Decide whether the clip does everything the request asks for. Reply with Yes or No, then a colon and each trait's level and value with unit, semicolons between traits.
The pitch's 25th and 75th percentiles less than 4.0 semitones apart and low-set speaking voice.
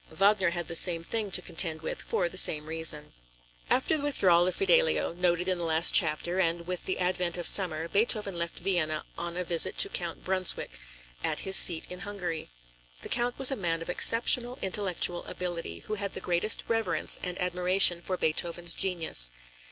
No: narrow, 2.6 semitones; medium, 180 Hz